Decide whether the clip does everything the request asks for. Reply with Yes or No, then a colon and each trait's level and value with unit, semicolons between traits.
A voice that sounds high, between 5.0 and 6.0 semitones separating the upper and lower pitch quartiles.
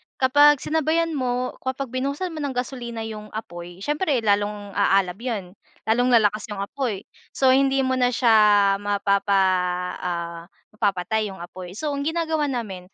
Yes: high, 235 Hz; average, 5.3 semitones